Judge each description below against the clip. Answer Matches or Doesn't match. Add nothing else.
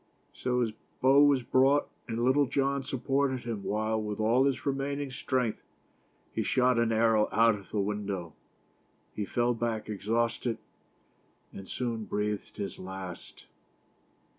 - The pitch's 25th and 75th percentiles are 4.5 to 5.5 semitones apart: Doesn't match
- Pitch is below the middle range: Matches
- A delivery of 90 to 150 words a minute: Matches